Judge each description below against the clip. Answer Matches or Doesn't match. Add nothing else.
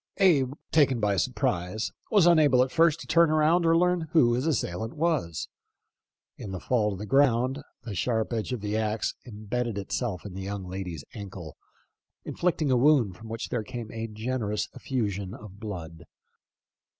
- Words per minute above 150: Matches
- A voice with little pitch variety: Doesn't match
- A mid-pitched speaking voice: Doesn't match